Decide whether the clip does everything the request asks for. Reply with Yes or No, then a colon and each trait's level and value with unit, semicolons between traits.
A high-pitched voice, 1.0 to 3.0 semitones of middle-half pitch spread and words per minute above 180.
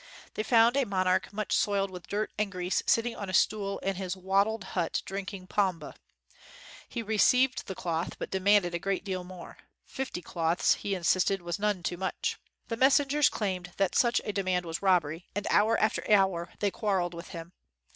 Yes: high, 195 Hz; average, 2.7 semitones; average, 195 wpm